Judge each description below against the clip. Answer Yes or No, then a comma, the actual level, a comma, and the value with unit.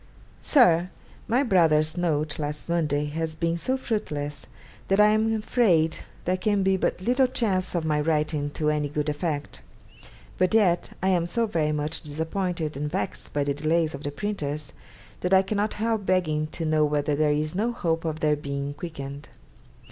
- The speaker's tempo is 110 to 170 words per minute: No, average, 180 wpm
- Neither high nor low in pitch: Yes, medium, 160 Hz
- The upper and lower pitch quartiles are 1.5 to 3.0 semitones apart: No, average, 4.2 semitones